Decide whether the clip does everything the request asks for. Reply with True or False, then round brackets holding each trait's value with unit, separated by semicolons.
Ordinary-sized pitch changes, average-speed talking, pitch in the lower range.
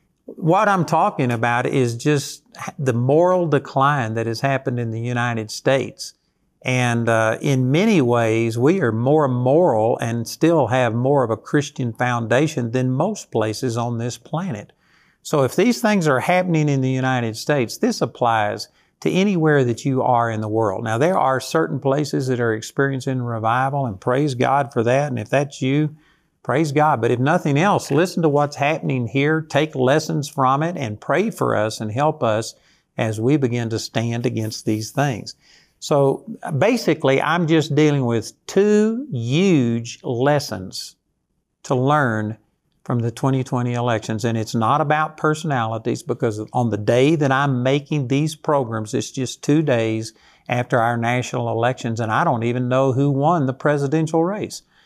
True (4.1 semitones; 170 wpm; 130 Hz)